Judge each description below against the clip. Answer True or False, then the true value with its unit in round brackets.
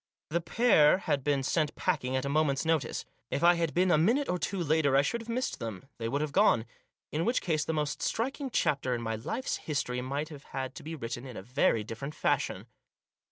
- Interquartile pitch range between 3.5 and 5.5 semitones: True (4.5 semitones)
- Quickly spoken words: True (225 wpm)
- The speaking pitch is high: False (150 Hz)